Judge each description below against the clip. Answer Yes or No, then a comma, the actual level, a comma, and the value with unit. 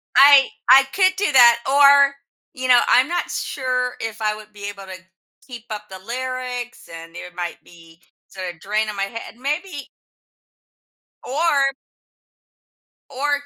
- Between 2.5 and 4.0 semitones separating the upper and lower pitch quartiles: No, average, 5.3 semitones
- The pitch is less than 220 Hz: No, very high, 250 Hz